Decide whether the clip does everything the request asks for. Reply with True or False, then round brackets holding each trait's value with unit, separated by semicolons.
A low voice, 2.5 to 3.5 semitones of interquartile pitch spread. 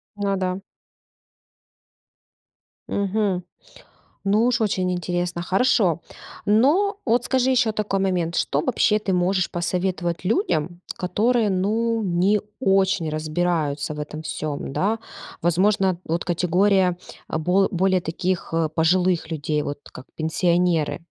False (185 Hz; 3.2 semitones)